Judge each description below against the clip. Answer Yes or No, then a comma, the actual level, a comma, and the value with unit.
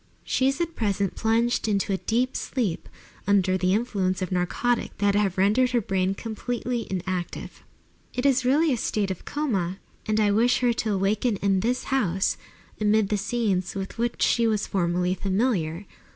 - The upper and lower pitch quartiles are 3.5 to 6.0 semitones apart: Yes, average, 4.1 semitones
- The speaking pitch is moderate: No, high, 210 Hz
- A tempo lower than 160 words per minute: No, average, 170 wpm